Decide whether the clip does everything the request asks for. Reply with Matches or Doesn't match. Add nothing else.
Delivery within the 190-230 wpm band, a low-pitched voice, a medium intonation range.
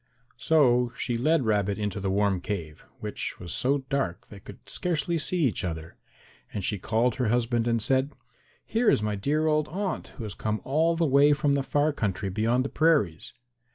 Doesn't match